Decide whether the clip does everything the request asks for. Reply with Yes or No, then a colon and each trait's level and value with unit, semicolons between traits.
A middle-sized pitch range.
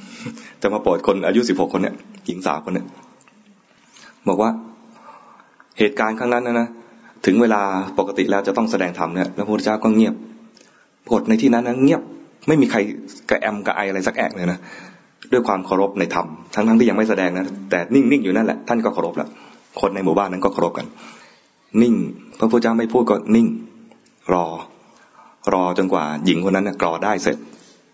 Yes: average, 4.4 semitones